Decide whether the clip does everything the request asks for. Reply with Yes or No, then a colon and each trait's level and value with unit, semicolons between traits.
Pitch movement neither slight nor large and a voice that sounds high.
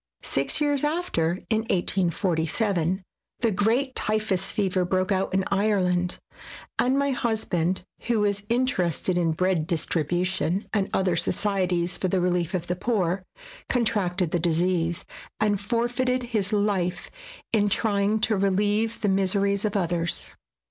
Yes: average, 3.3 semitones; high, 195 Hz